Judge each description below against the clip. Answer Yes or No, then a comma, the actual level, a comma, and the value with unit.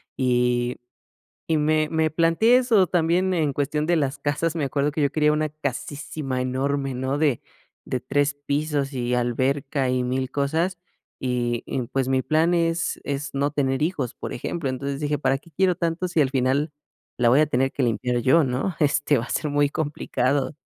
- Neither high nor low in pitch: Yes, medium, 145 Hz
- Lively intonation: No, average, 3.1 semitones